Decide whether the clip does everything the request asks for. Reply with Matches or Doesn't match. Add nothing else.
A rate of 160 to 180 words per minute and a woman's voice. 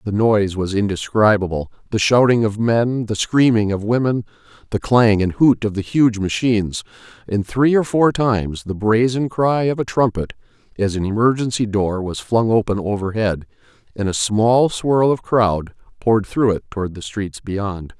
Doesn't match